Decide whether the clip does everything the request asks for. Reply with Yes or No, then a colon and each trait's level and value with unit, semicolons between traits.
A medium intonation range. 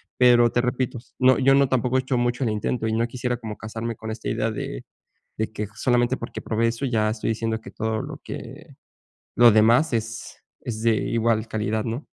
No: narrow, 1.8 semitones